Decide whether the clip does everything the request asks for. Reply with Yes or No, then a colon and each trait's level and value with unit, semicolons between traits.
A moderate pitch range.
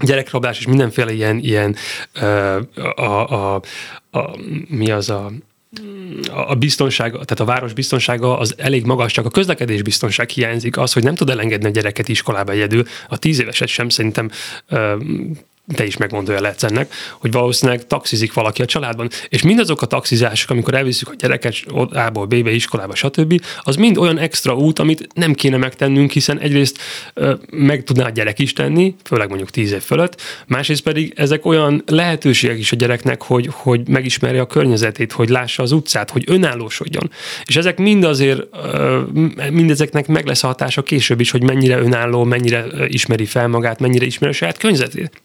Yes: average, 4.2 semitones